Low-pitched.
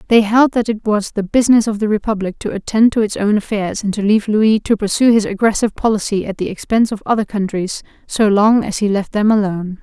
No: high, 210 Hz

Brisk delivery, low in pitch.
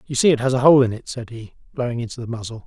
Yes: fast, 315 wpm; low, 120 Hz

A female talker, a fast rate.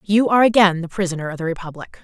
Yes: female; fast, 235 wpm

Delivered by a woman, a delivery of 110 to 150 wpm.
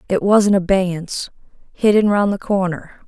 Yes: female; slow, 135 wpm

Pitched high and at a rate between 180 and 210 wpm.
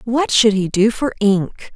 Yes: high, 220 Hz; fast, 205 wpm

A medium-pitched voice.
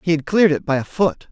Yes: medium, 165 Hz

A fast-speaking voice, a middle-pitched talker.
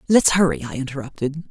No: average, 160 wpm; medium, 145 Hz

